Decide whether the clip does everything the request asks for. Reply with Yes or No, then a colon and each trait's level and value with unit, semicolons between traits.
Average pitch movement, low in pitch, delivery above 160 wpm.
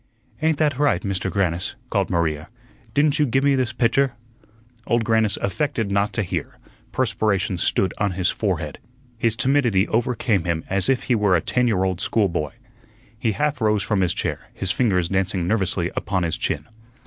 Yes: average, 4.8 semitones; low, 105 Hz; average, 175 wpm